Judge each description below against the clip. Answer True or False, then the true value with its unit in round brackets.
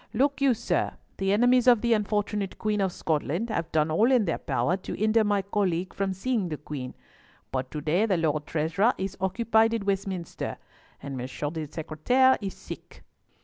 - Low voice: False (195 Hz)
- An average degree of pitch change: False (5.7 semitones)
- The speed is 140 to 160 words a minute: False (185 wpm)